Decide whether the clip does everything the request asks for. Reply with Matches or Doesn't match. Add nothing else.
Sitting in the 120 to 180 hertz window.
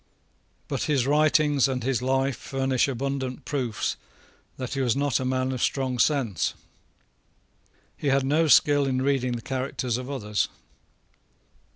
Matches